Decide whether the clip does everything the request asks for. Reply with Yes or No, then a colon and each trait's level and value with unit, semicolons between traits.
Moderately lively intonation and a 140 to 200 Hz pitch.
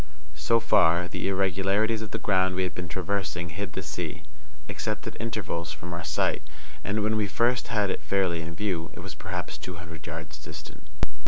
No: average, 3.4 semitones; very low, 95 Hz